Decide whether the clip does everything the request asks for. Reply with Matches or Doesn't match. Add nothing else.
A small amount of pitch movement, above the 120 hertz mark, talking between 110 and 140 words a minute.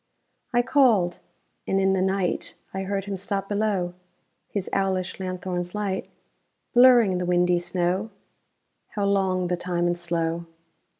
Matches